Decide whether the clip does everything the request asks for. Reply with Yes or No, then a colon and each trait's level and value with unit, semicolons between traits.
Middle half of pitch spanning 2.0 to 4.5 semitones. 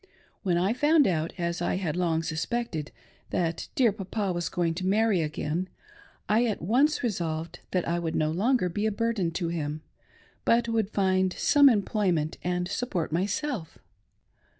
No: average, 5.0 semitones